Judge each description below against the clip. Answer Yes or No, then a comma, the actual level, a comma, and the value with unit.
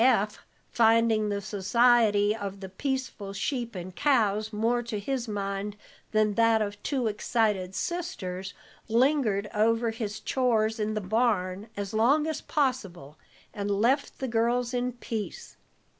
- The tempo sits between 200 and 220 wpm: No, average, 140 wpm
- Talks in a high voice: Yes, high, 220 Hz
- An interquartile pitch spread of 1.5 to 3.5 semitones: Yes, average, 3.1 semitones